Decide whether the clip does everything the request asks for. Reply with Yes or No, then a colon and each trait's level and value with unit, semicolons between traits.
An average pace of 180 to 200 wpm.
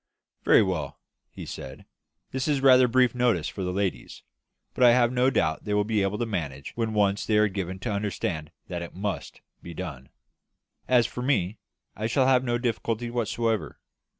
Yes: average, 185 wpm